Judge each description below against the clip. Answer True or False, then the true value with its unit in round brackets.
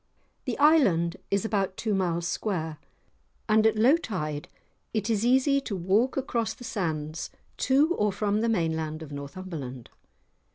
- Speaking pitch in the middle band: False (200 Hz)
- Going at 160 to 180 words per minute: False (150 wpm)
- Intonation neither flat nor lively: False (5.9 semitones)